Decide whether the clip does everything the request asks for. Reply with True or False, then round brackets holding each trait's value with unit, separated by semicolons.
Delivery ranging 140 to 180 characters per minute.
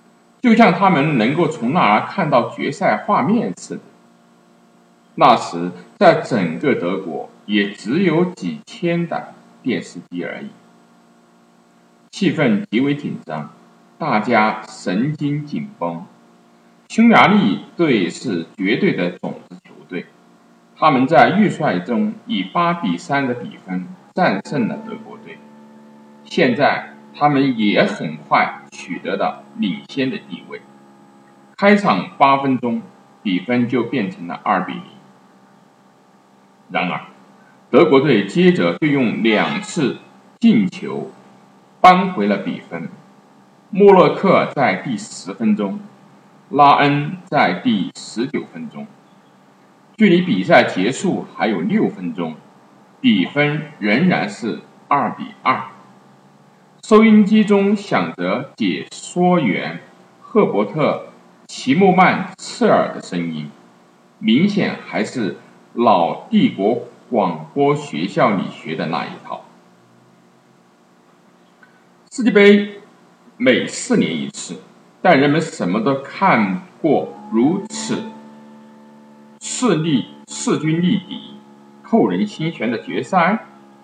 True (165 characters per minute)